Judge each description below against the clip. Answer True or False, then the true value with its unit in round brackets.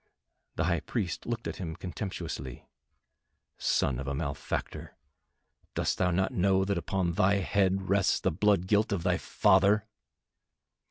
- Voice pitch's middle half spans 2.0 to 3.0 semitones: True (2.7 semitones)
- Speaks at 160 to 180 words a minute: False (145 wpm)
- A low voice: True (95 Hz)